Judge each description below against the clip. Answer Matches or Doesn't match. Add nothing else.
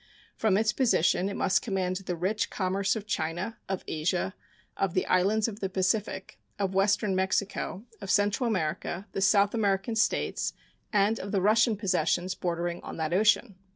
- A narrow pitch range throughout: Matches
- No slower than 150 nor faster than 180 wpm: Matches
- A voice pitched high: Matches